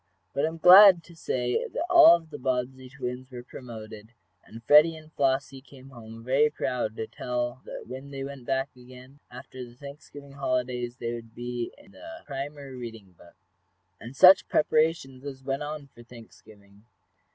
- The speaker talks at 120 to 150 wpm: No, average, 175 wpm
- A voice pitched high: No, low, 130 Hz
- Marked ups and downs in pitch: No, average, 2.9 semitones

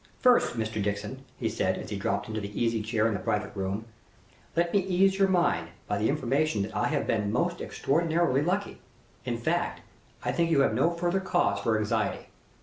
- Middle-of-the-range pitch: No, low, 130 Hz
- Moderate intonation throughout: No, wide, 8.1 semitones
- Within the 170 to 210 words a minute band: Yes, average, 200 wpm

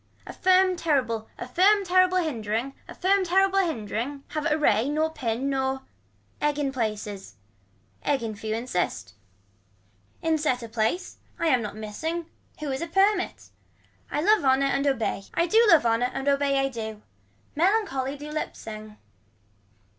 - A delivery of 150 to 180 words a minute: Yes, average, 155 wpm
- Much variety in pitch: Yes, wide, 6.4 semitones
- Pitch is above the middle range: Yes, very high, 275 Hz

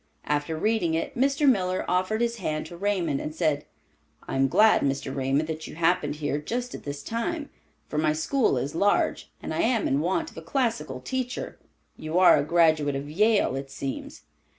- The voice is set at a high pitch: No, medium, 165 Hz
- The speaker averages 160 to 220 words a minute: Yes, average, 195 wpm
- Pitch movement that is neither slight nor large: No, wide, 7.1 semitones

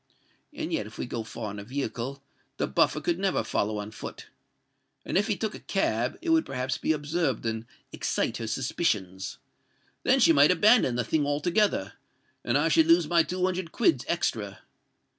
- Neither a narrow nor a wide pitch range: No, wide, 7.8 semitones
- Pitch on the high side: No, medium, 145 Hz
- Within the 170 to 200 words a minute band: Yes, average, 185 wpm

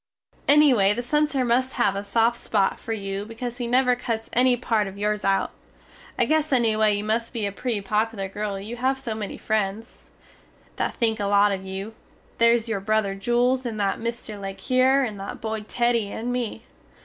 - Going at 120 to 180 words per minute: No, average, 195 wpm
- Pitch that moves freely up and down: No, average, 3.1 semitones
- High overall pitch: Yes, high, 225 Hz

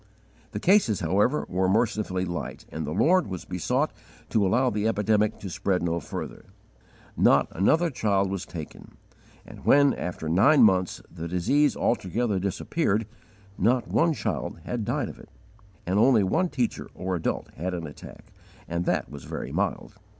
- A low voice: Yes, low, 100 Hz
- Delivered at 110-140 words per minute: No, average, 165 wpm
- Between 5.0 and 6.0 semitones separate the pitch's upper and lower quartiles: Yes, average, 5.3 semitones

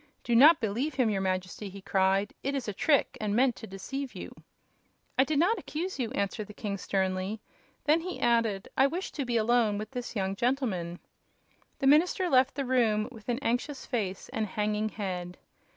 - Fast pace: No, average, 190 wpm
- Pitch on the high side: Yes, high, 230 Hz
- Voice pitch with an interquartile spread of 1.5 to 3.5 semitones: No, average, 5.2 semitones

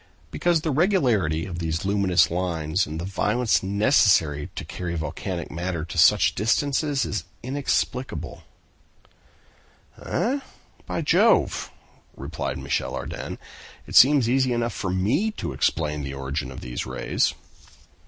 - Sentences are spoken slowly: Yes, slow, 130 wpm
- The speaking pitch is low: Yes, very low, 95 Hz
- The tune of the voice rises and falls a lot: Yes, wide, 7.7 semitones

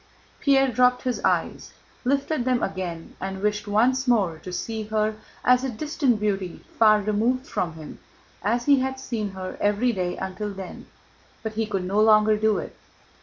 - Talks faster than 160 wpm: Yes, average, 170 wpm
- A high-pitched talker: Yes, high, 215 Hz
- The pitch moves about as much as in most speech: Yes, average, 4.3 semitones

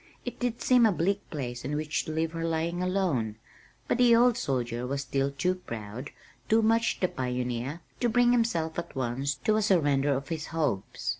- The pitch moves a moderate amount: No, wide, 7.2 semitones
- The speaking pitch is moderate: Yes, medium, 160 Hz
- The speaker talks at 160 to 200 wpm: Yes, average, 195 wpm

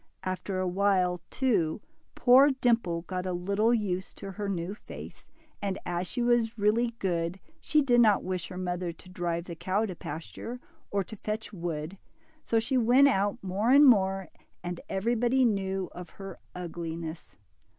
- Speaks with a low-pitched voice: No, high, 195 Hz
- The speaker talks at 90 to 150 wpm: No, average, 165 wpm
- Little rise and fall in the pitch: No, average, 4.3 semitones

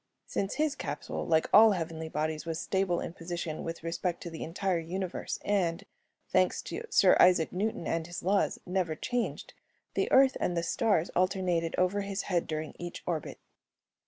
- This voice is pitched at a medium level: Yes, medium, 175 Hz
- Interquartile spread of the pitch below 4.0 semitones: Yes, average, 2.8 semitones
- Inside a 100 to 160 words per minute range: No, average, 170 wpm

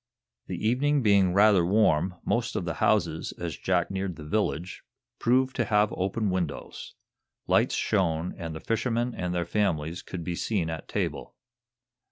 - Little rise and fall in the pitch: No, average, 4.1 semitones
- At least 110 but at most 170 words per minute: Yes, average, 160 wpm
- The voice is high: No, very low, 95 Hz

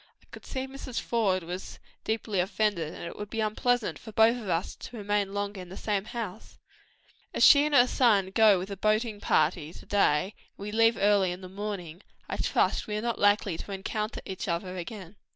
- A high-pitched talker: Yes, high, 205 Hz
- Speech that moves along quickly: Yes, fast, 210 wpm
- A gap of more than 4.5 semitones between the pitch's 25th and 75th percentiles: No, average, 2.9 semitones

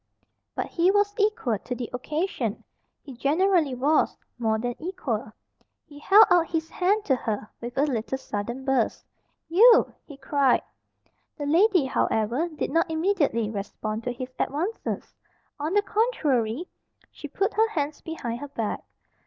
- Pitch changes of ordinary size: No, wide, 6.7 semitones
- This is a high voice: Yes, very high, 290 Hz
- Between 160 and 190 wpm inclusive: No, average, 150 wpm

